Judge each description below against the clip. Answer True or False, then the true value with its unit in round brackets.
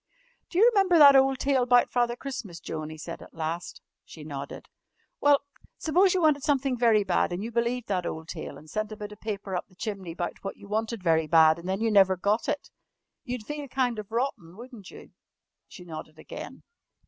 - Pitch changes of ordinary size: False (6.8 semitones)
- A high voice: True (215 Hz)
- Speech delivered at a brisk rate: True (210 wpm)